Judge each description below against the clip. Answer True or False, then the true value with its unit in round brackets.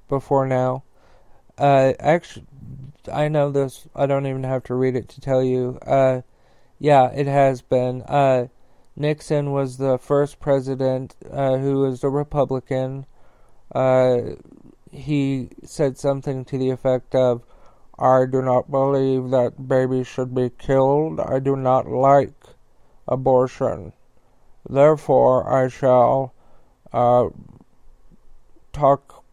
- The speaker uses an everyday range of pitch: False (1.5 semitones)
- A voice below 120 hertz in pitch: False (135 Hz)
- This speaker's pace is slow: True (125 wpm)